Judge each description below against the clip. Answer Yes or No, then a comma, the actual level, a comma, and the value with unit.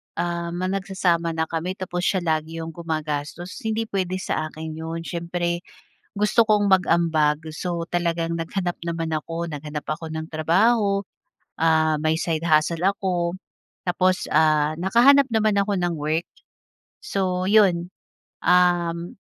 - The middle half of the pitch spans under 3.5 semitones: Yes, narrow, 2.6 semitones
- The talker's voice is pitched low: No, medium, 170 Hz